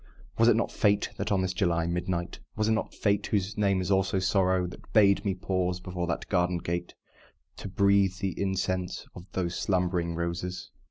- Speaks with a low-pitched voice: Yes, very low, 95 Hz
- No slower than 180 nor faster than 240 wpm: Yes, average, 185 wpm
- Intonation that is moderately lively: No, narrow, 1.9 semitones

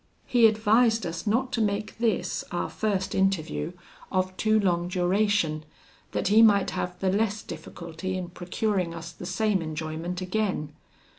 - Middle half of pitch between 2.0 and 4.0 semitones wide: Yes, average, 3.6 semitones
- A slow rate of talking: No, average, 150 wpm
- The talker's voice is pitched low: No, high, 190 Hz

